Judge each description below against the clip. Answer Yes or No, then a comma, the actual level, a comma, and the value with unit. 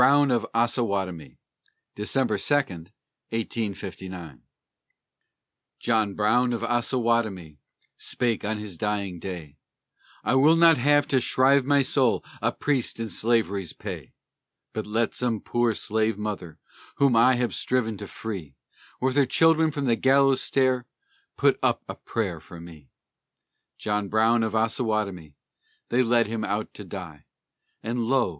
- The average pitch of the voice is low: Yes, low, 115 Hz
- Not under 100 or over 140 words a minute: Yes, slow, 135 wpm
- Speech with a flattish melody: No, average, 4.3 semitones